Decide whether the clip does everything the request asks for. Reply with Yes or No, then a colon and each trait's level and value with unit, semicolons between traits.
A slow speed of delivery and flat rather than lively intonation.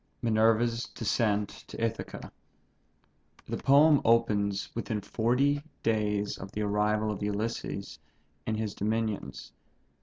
Yes: slow, 115 wpm; narrow, 2.0 semitones